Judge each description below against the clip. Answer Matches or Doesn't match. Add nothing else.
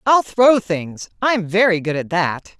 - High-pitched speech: Matches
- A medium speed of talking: Matches